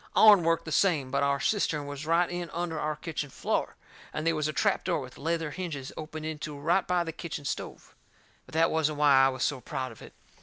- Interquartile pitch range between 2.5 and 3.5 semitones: Yes, average, 2.9 semitones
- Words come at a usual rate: No, fast, 235 wpm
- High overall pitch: No, medium, 155 Hz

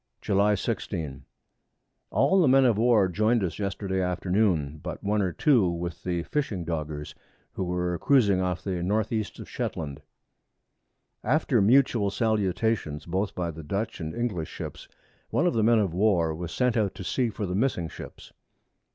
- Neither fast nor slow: Yes, average, 170 wpm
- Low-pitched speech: Yes, very low, 95 Hz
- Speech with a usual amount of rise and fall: Yes, average, 4.2 semitones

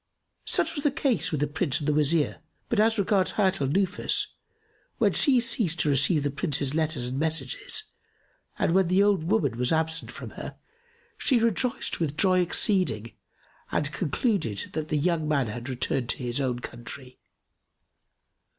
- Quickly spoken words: No, average, 170 wpm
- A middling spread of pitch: No, wide, 5.7 semitones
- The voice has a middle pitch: Yes, medium, 160 Hz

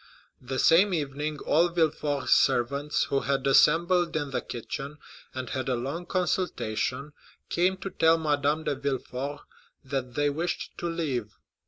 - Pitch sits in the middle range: Yes, medium, 145 Hz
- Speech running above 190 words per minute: No, average, 145 wpm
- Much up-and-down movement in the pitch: No, average, 3.7 semitones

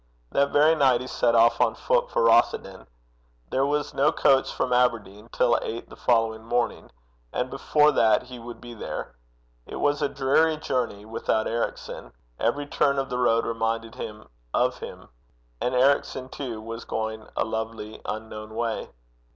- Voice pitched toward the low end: Yes, low, 120 Hz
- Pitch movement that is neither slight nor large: Yes, average, 3.6 semitones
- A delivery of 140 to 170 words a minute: Yes, average, 165 wpm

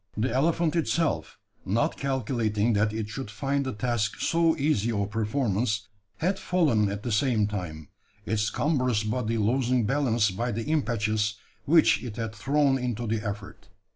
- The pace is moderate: Yes, average, 155 wpm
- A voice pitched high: No, low, 115 Hz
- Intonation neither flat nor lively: Yes, average, 4.3 semitones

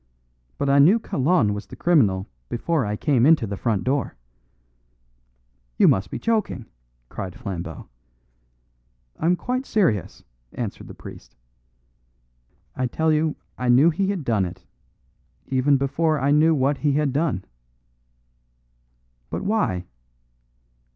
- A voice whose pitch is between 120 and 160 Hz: Yes, medium, 140 Hz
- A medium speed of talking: No, slow, 130 wpm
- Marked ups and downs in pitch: Yes, wide, 6.7 semitones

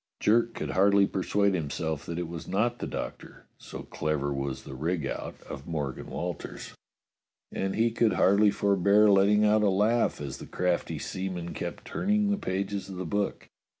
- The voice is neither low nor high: No, very low, 95 Hz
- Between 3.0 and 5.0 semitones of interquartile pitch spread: Yes, average, 3.8 semitones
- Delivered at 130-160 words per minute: No, average, 175 wpm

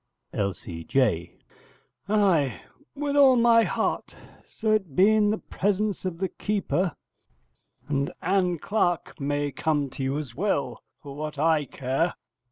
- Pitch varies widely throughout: Yes, wide, 6.8 semitones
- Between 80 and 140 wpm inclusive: Yes, slow, 135 wpm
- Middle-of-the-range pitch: Yes, medium, 165 Hz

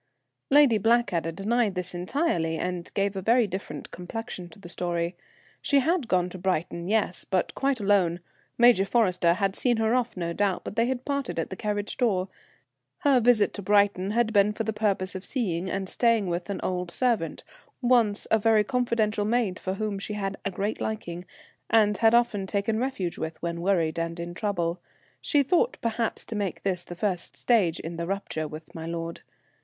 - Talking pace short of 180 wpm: No, average, 190 wpm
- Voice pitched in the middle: No, high, 200 Hz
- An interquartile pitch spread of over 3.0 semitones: Yes, average, 4.2 semitones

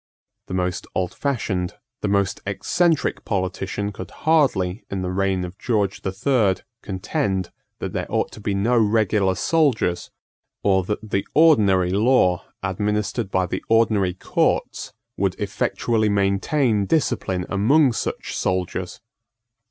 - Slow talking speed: Yes, slow, 130 wpm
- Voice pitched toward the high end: No, low, 100 Hz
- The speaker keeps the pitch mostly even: No, average, 3.3 semitones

